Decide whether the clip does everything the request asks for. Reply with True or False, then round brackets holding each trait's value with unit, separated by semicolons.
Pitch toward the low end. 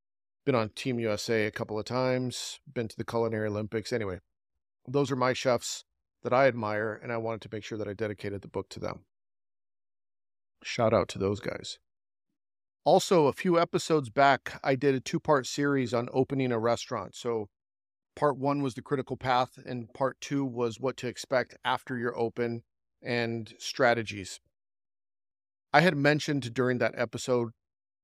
True (120 Hz)